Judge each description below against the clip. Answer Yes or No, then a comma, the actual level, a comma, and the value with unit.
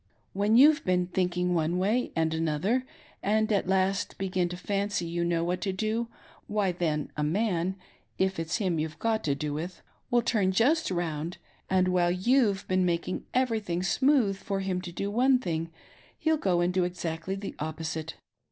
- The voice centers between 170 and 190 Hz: Yes, medium, 185 Hz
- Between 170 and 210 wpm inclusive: Yes, average, 180 wpm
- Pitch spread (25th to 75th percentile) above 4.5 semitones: No, average, 3.5 semitones